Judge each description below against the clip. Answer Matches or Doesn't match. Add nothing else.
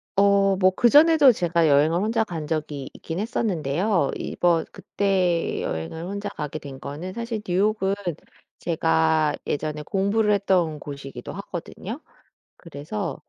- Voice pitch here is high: Doesn't match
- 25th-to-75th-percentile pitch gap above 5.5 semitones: Doesn't match